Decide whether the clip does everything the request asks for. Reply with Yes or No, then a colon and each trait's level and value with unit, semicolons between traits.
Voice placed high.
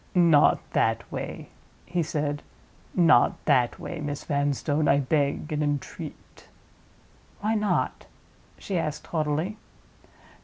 No: medium, 150 Hz